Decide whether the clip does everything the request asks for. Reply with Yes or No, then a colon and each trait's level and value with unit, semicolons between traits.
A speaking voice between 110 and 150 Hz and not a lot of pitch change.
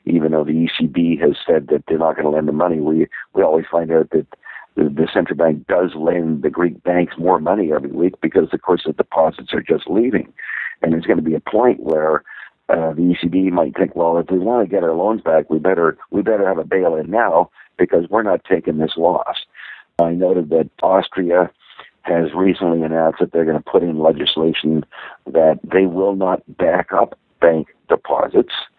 No: very low, 85 Hz; narrow, 1.8 semitones